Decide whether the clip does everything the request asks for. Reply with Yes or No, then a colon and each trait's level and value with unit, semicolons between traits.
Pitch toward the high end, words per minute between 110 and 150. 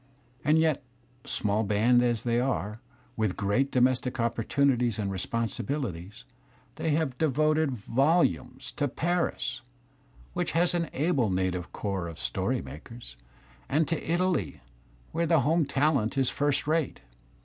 No: low, 125 Hz; slow, 135 wpm